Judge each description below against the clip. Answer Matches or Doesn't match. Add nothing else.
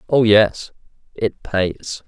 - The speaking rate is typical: Doesn't match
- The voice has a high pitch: Doesn't match